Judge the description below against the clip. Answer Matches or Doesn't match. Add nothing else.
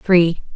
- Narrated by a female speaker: Matches